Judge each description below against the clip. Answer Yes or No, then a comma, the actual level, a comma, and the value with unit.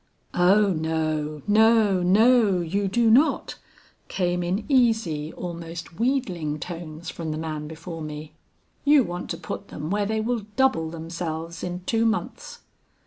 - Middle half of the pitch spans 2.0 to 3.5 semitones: No, wide, 5.4 semitones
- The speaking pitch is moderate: Yes, medium, 175 Hz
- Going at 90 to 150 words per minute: Yes, average, 140 wpm